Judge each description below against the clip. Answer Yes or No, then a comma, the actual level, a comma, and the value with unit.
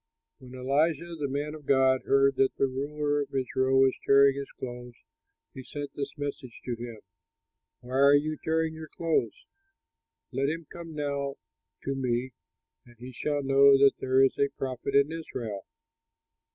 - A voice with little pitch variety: Yes, narrow, 2.0 semitones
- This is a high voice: No, medium, 140 Hz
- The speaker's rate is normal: Yes, average, 165 wpm